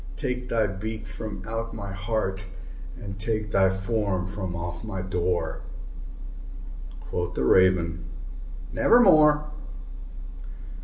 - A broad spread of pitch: No, average, 3.4 semitones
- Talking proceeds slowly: Yes, slow, 105 wpm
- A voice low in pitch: Yes, low, 100 Hz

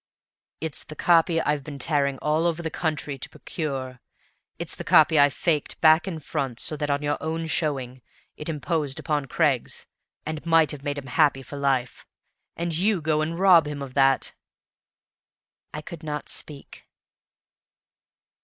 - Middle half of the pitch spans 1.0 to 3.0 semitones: Yes, narrow, 2.5 semitones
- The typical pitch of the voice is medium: Yes, medium, 150 Hz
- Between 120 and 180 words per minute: Yes, average, 165 wpm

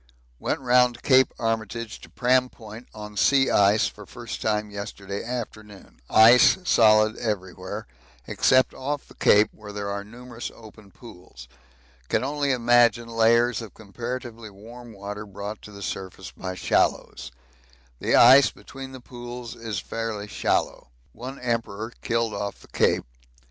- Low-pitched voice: Yes, low, 115 Hz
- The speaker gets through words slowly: No, average, 145 wpm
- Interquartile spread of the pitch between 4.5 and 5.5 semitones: No, average, 2.9 semitones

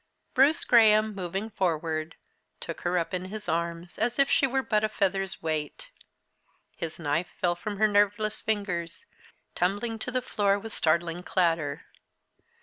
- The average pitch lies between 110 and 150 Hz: No, high, 195 Hz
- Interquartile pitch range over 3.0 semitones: Yes, average, 4.2 semitones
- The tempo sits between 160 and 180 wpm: No, average, 150 wpm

